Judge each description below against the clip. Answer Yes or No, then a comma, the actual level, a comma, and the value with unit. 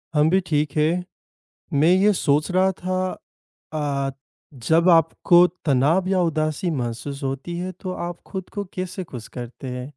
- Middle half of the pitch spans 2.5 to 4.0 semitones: No, average, 4.6 semitones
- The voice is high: No, medium, 165 Hz